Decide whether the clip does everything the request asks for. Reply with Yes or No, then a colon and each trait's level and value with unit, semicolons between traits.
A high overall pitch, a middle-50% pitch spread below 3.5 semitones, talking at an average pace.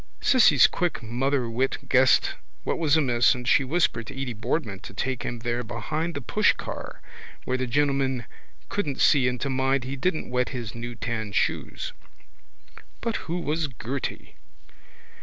No: low, 130 Hz; average, 3.1 semitones; average, 155 wpm